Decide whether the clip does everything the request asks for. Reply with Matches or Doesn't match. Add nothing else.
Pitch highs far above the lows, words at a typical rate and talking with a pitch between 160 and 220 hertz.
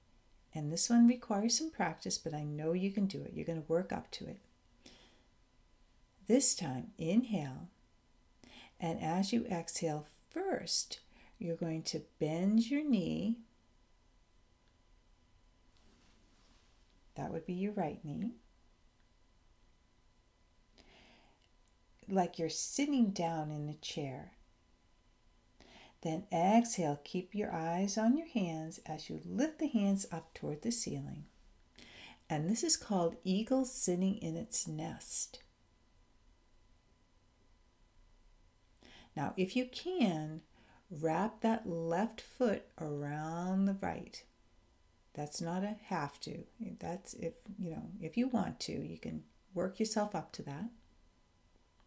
Doesn't match